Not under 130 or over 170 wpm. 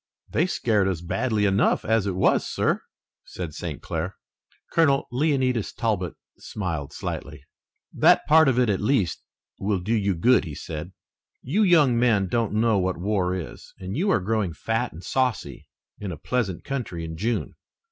Yes: average, 165 wpm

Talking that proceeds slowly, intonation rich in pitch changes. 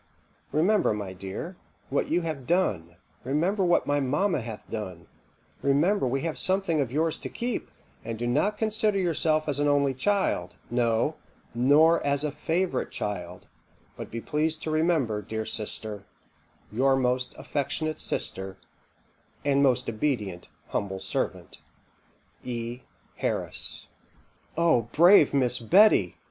Yes: slow, 130 wpm; wide, 6.3 semitones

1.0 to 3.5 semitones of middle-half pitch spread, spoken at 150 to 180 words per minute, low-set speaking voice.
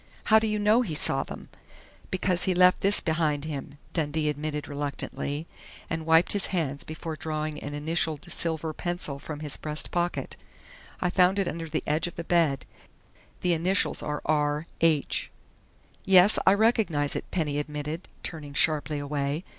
No: average, 3.2 semitones; average, 160 wpm; medium, 160 Hz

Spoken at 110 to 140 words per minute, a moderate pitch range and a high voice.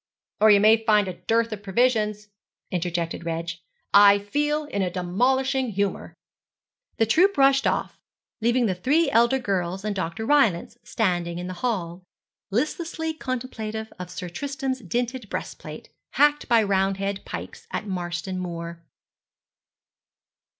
No: slow, 135 wpm; wide, 5.8 semitones; high, 210 Hz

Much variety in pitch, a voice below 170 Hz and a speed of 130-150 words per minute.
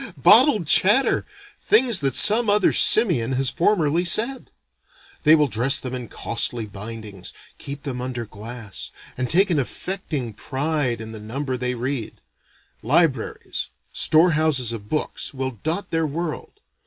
Yes: wide, 6.1 semitones; medium, 140 Hz; average, 140 wpm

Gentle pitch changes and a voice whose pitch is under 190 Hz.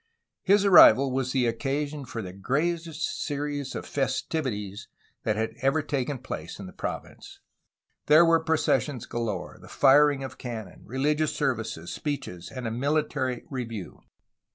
No: average, 4.6 semitones; low, 135 Hz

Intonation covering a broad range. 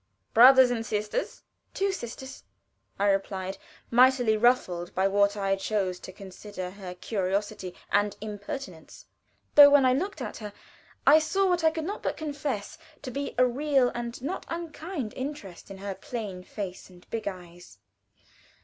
Yes: wide, 6.1 semitones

